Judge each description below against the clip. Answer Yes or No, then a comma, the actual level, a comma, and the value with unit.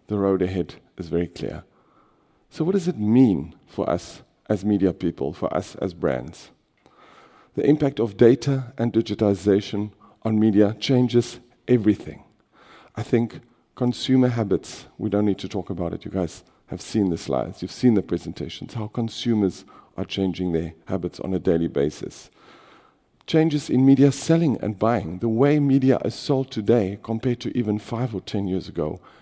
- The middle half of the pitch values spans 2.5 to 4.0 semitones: No, average, 4.7 semitones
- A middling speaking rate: Yes, average, 165 wpm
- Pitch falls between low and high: No, low, 105 Hz